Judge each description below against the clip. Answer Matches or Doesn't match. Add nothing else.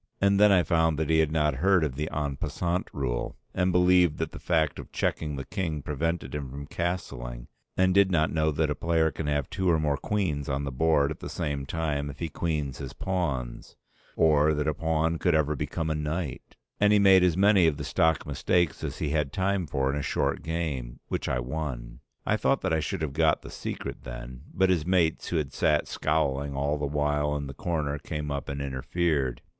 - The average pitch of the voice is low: Matches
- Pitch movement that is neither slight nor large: Matches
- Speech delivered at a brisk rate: Matches